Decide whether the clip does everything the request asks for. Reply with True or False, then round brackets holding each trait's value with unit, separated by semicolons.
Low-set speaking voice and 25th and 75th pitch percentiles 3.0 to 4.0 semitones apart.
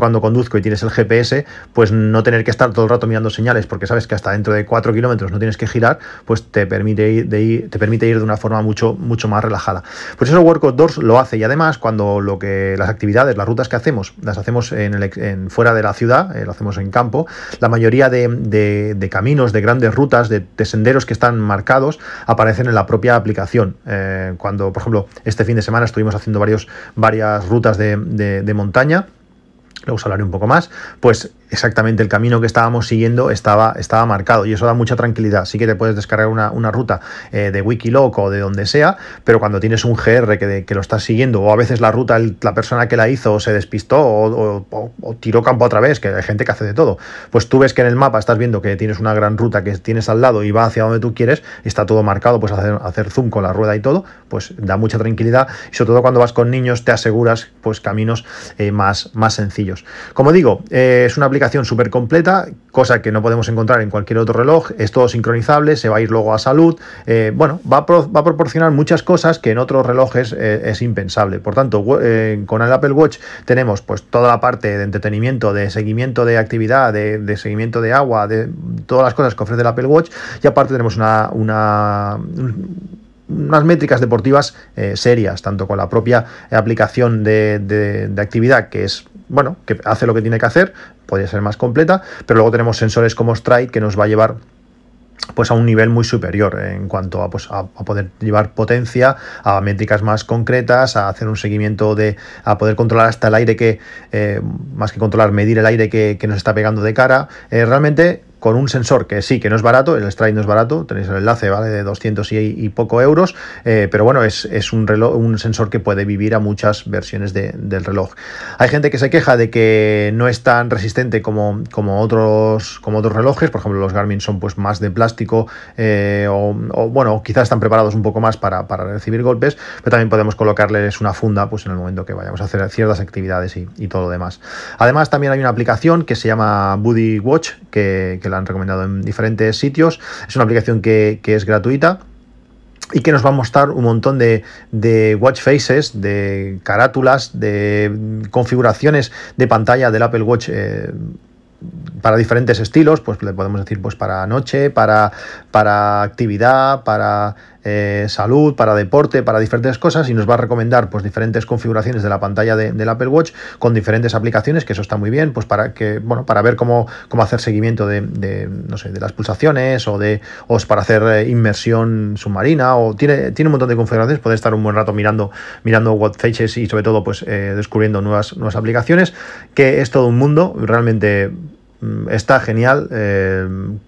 False (110 Hz; 2.6 semitones)